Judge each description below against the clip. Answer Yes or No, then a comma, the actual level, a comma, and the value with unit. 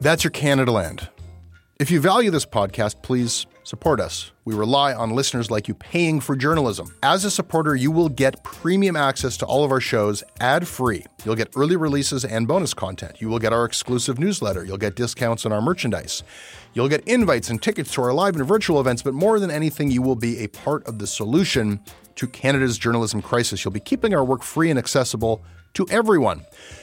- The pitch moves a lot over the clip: Yes, wide, 5.7 semitones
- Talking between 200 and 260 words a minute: Yes, fast, 205 wpm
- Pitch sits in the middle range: No, low, 125 Hz